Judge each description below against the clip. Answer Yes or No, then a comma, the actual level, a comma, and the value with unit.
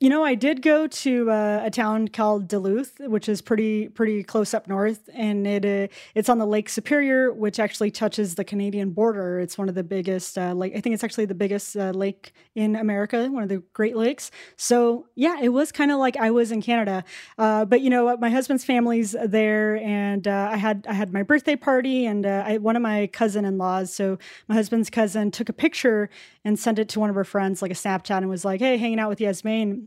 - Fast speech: Yes, fast, 235 wpm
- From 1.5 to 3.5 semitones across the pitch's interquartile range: Yes, average, 2.7 semitones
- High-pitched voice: Yes, high, 215 Hz